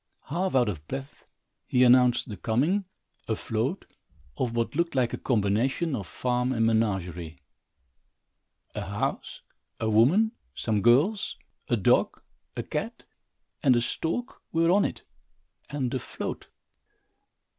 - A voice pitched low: Yes, low, 125 Hz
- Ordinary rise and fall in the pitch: Yes, average, 4.9 semitones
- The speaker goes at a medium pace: No, slow, 125 wpm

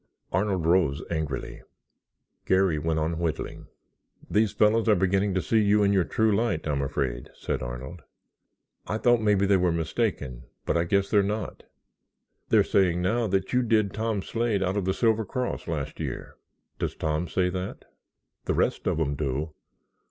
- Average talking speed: Yes, average, 170 wpm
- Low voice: Yes, very low, 95 Hz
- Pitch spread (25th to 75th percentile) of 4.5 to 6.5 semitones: Yes, average, 4.8 semitones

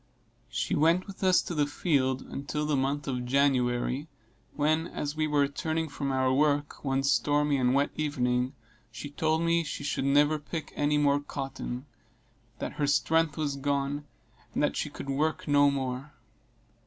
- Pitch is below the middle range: No, medium, 145 Hz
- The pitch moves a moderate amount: No, narrow, 1.8 semitones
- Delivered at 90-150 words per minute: No, average, 165 wpm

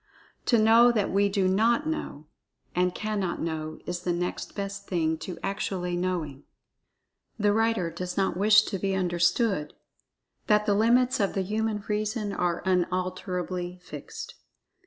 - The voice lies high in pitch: Yes, high, 195 Hz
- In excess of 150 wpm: No, average, 145 wpm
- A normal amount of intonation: Yes, average, 3.2 semitones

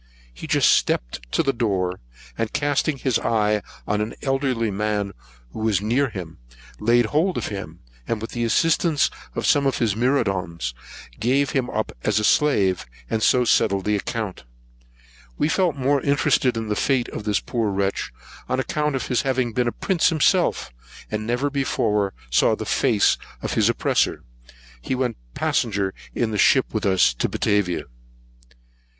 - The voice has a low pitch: Yes, low, 115 Hz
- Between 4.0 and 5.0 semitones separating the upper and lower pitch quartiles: Yes, average, 4.7 semitones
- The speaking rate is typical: Yes, average, 170 wpm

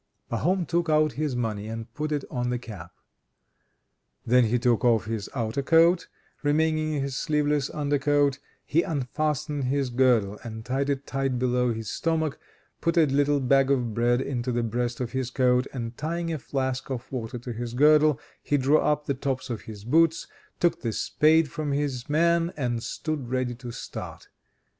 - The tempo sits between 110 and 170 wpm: No, average, 180 wpm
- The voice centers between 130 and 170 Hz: Yes, low, 135 Hz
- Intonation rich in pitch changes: No, average, 3.8 semitones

